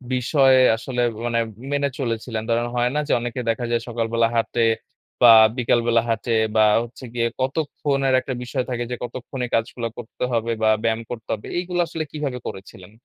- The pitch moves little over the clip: Yes, narrow, 2.3 semitones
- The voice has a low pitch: Yes, low, 120 Hz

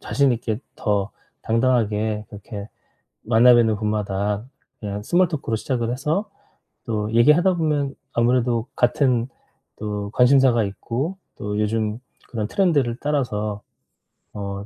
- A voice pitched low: Yes, low, 115 Hz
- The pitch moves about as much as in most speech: Yes, average, 3.9 semitones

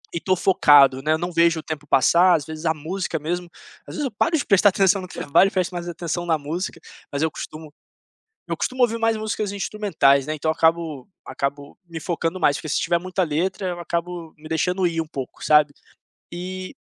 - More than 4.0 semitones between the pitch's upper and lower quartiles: No, average, 3.2 semitones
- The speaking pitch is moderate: Yes, medium, 170 Hz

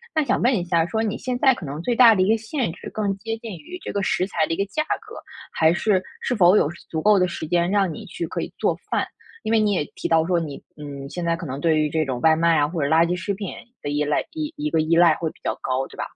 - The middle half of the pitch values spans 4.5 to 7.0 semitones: Yes, average, 5.2 semitones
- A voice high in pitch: No, medium, 175 Hz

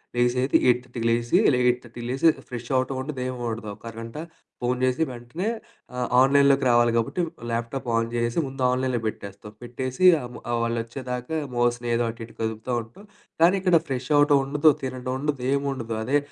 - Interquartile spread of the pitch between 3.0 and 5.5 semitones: No, narrow, 2.4 semitones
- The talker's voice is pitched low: Yes, low, 125 Hz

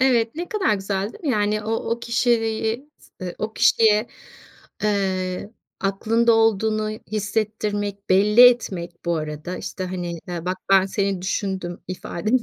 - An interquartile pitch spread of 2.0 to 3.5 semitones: Yes, average, 3.1 semitones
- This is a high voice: Yes, high, 210 Hz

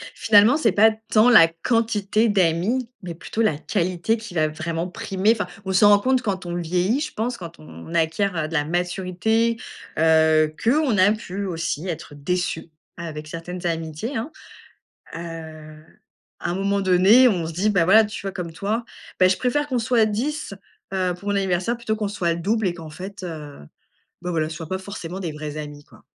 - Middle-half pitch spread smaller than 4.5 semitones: No, average, 4.8 semitones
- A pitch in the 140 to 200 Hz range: Yes, medium, 185 Hz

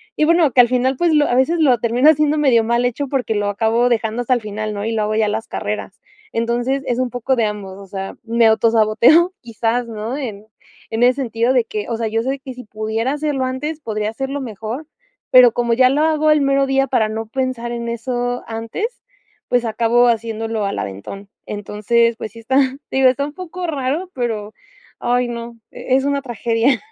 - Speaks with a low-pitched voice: No, high, 240 Hz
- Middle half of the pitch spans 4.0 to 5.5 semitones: No, average, 3.2 semitones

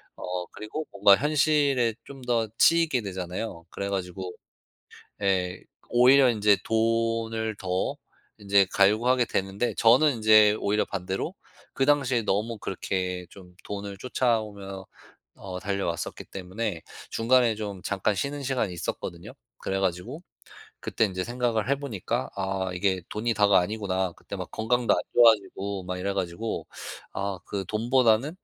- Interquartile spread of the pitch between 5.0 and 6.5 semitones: No, average, 3.8 semitones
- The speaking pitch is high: No, low, 105 Hz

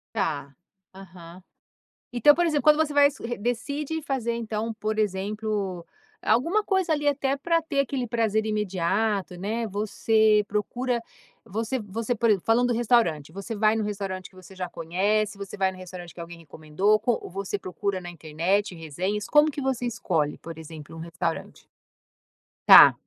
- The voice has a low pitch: No, high, 210 Hz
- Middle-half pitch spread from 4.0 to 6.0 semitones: Yes, average, 4.6 semitones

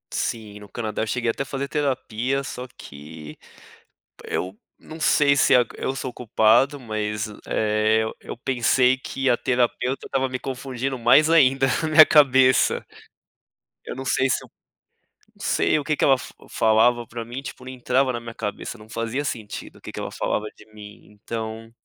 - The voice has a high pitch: No, low, 120 Hz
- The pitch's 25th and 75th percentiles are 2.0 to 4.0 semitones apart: Yes, average, 3.4 semitones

